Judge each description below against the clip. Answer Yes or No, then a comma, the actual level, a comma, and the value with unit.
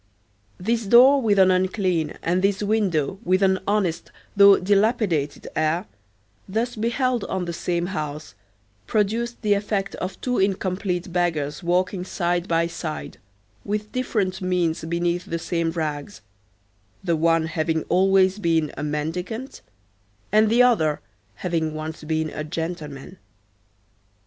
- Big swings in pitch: No, average, 3.9 semitones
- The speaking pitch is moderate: Yes, medium, 180 Hz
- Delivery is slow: Yes, slow, 130 wpm